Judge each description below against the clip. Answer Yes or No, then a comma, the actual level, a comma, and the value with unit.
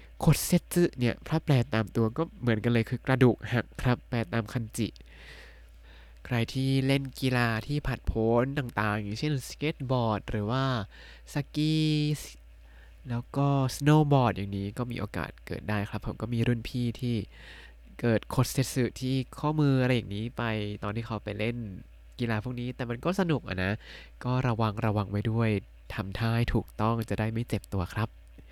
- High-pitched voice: No, low, 115 Hz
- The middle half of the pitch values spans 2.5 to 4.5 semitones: Yes, average, 3.6 semitones